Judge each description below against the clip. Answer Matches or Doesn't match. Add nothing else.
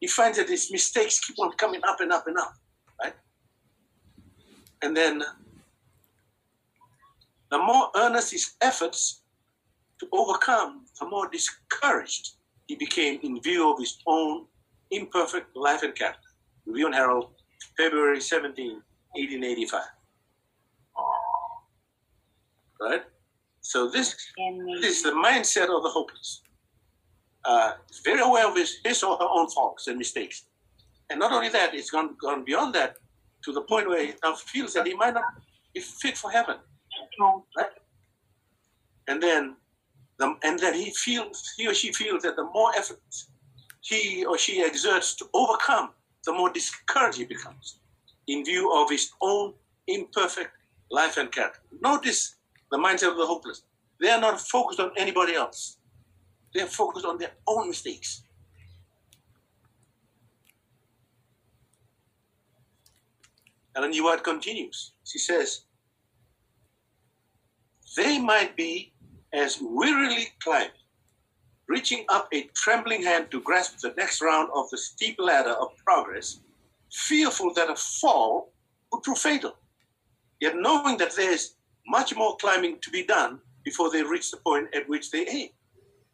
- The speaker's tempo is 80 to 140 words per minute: Matches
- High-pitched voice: Doesn't match